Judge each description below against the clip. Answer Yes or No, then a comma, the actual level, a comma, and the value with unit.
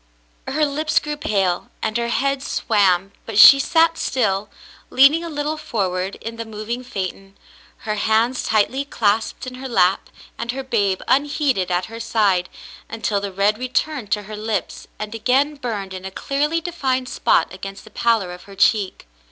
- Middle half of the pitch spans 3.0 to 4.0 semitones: No, average, 5.2 semitones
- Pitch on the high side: Yes, high, 225 Hz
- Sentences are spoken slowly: No, average, 170 wpm